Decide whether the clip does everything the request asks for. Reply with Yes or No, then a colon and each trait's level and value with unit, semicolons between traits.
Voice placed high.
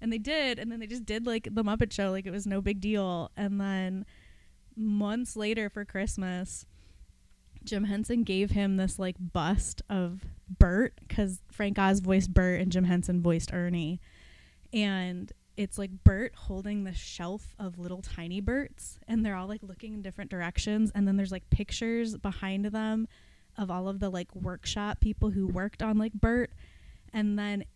Yes: high, 195 Hz